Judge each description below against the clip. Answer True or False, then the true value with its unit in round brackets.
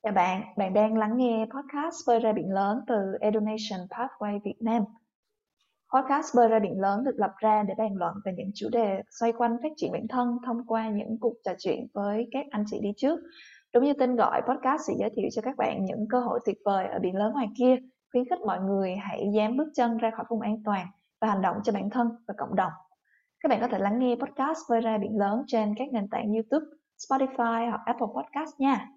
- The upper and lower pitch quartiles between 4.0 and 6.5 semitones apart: False (3.6 semitones)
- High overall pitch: True (225 Hz)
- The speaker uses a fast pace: False (235 wpm)